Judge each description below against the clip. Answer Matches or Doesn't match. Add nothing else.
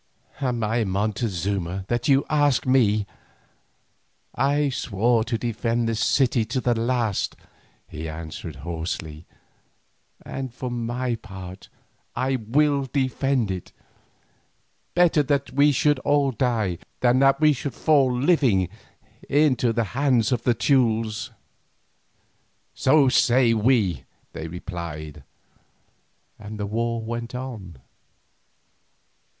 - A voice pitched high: Doesn't match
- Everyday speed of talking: Doesn't match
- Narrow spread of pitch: Doesn't match